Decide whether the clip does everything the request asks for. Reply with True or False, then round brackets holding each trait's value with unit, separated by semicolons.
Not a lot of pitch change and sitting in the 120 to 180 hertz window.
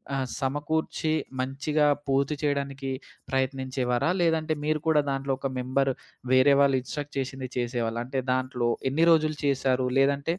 True (2.1 semitones; 135 Hz)